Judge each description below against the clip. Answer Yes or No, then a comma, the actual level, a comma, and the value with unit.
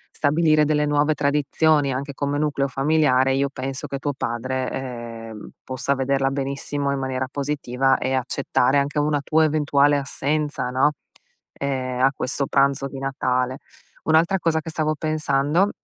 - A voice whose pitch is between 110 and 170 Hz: Yes, medium, 140 Hz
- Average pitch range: No, narrow, 1.9 semitones